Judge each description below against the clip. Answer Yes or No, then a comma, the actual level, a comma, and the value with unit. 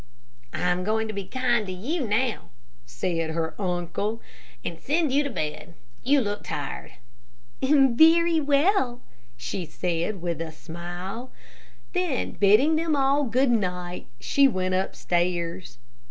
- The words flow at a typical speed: No, slow, 130 wpm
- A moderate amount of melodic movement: No, wide, 7.6 semitones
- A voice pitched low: No, high, 210 Hz